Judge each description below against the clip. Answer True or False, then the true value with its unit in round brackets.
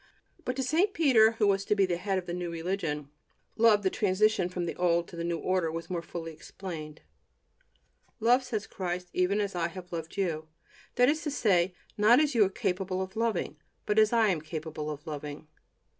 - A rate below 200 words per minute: False (205 wpm)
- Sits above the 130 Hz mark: True (185 Hz)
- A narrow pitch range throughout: False (4.2 semitones)